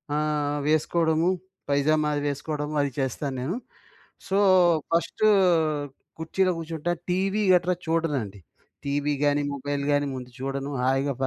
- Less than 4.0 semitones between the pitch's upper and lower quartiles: Yes, average, 2.9 semitones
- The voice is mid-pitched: Yes, medium, 145 Hz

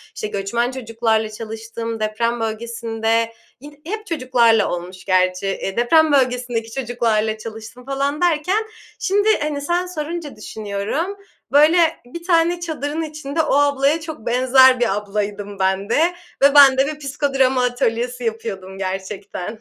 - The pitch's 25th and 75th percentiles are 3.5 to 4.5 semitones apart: No, average, 5.2 semitones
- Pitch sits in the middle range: No, high, 245 Hz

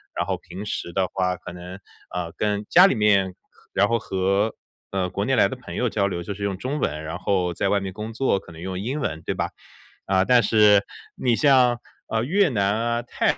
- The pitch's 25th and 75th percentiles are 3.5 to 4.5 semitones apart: Yes, average, 4.0 semitones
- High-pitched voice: No, low, 100 Hz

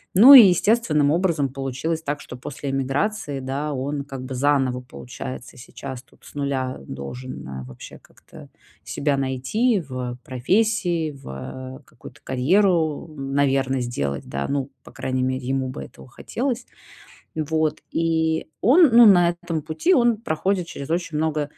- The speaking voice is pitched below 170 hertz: Yes, medium, 140 Hz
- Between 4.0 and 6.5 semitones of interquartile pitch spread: Yes, average, 4.5 semitones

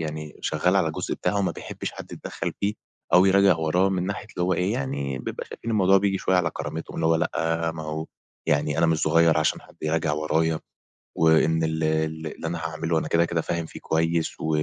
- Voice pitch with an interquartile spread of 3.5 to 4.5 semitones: No, narrow, 2.4 semitones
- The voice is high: No, very low, 80 Hz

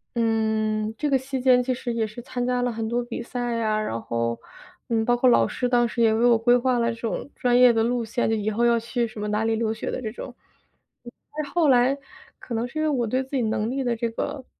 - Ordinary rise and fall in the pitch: No, narrow, 1.9 semitones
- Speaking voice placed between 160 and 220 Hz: No, high, 235 Hz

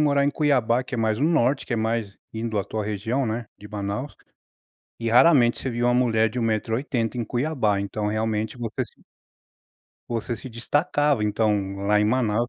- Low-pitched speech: Yes, low, 115 Hz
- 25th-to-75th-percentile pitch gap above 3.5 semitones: No, average, 2.9 semitones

